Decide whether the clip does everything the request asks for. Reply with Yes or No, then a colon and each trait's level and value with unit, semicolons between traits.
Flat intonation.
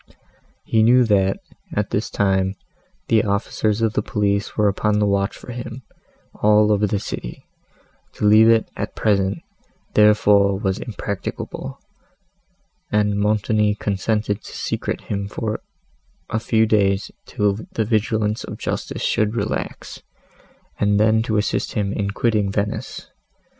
Yes: narrow, 1.4 semitones